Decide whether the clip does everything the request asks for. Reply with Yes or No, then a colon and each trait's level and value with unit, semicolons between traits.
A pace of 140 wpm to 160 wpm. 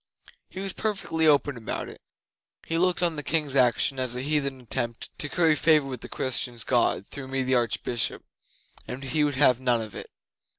No: average, 195 wpm